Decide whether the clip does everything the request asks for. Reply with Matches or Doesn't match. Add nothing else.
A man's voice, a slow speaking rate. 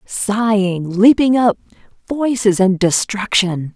Doesn't match